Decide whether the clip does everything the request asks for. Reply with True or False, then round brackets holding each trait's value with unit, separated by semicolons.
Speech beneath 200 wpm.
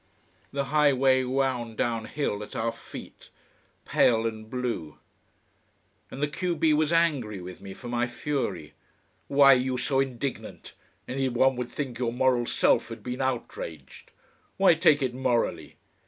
True (155 wpm)